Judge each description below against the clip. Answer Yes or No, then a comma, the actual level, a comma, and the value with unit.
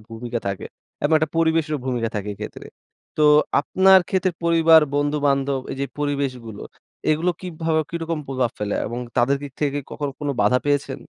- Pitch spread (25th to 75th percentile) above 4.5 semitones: No, average, 4.0 semitones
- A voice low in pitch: No, medium, 145 Hz